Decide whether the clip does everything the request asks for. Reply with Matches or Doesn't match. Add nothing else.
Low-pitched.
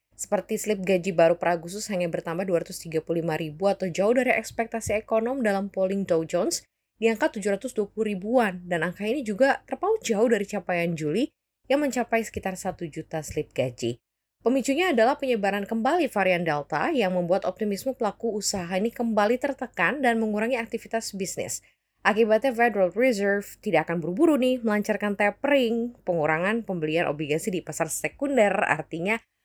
Doesn't match